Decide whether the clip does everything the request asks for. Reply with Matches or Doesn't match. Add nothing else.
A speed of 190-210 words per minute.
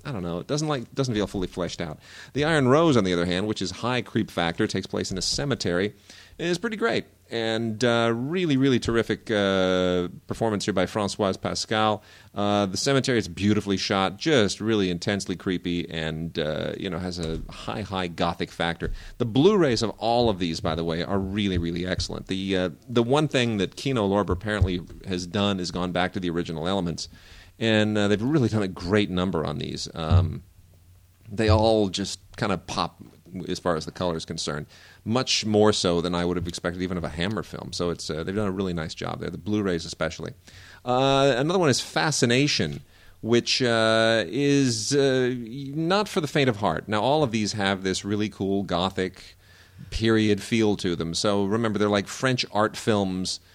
Matches